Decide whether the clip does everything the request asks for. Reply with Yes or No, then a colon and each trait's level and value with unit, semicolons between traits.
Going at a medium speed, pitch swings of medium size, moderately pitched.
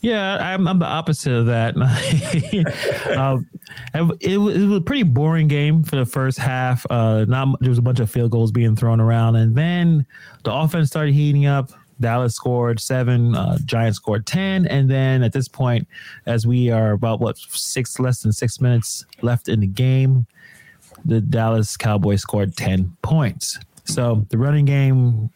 No: average, 175 wpm; average, 4.2 semitones; low, 125 Hz